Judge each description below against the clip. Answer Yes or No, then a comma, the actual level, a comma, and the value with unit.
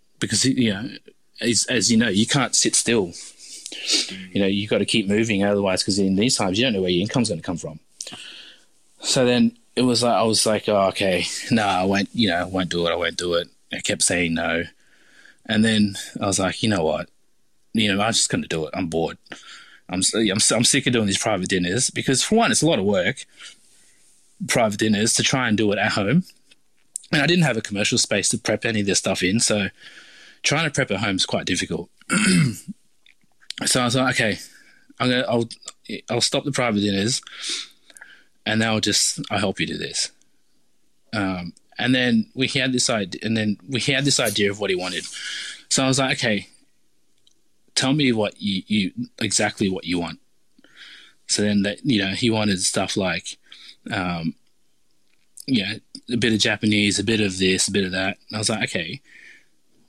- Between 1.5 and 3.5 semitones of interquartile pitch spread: No, average, 4.0 semitones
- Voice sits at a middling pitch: No, low, 110 Hz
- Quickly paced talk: Yes, fast, 210 wpm